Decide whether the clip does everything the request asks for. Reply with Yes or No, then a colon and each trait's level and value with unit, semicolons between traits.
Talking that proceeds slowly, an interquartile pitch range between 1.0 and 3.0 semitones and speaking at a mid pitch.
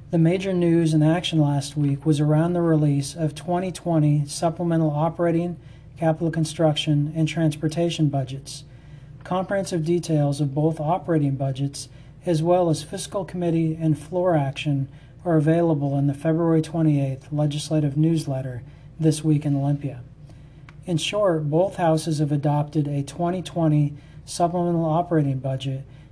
Yes: slow, 130 wpm; average, 2.7 semitones; medium, 155 Hz